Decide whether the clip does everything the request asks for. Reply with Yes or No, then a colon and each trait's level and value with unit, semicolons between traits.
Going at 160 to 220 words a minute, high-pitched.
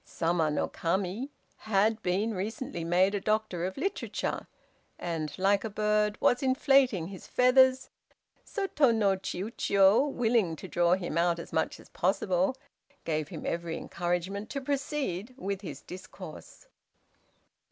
No: average, 140 wpm; high, 195 Hz